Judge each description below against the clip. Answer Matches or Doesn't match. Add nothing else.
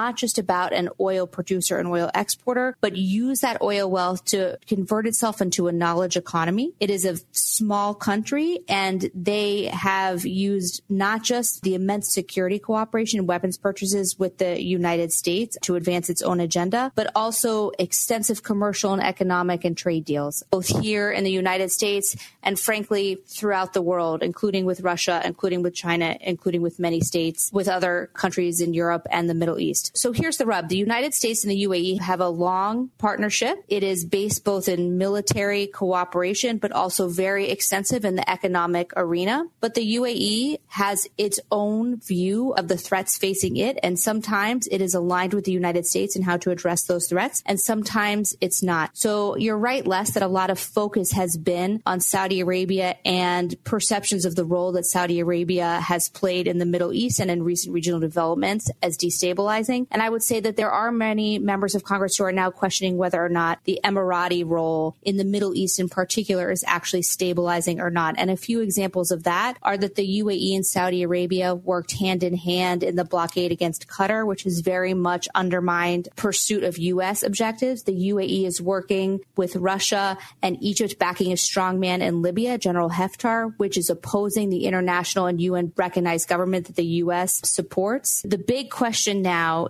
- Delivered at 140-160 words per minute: Doesn't match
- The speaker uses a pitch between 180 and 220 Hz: Matches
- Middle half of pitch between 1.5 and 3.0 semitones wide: Matches